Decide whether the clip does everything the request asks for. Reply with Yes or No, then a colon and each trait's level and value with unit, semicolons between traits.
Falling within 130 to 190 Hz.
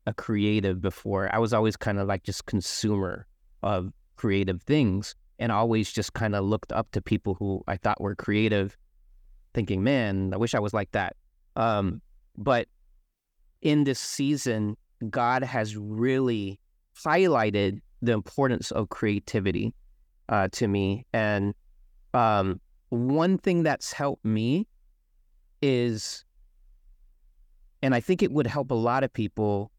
No: low, 105 Hz